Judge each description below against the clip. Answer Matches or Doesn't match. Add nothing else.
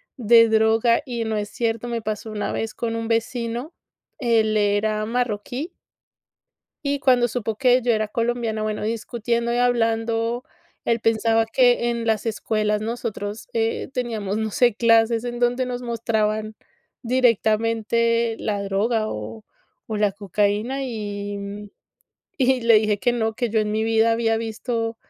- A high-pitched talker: Matches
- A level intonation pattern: Matches